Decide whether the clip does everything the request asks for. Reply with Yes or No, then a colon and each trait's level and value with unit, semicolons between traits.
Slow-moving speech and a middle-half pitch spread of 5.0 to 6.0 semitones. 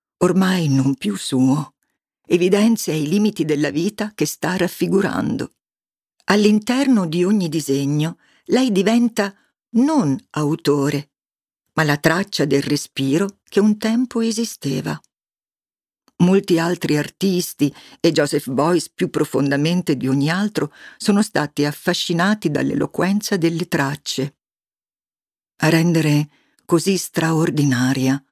Yes: slow, 105 wpm; wide, 5.6 semitones